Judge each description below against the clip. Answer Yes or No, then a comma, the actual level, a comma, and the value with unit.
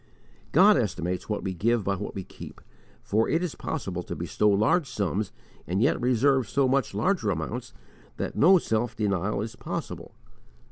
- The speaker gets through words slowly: No, average, 170 wpm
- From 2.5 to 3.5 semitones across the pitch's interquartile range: No, average, 5.2 semitones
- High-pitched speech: No, low, 110 Hz